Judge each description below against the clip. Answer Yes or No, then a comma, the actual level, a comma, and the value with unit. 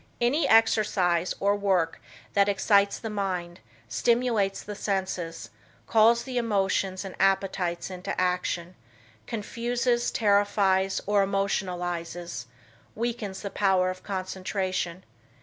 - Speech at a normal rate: No, slow, 105 wpm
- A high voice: Yes, high, 195 Hz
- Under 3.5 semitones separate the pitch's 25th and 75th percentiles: Yes, narrow, 2.4 semitones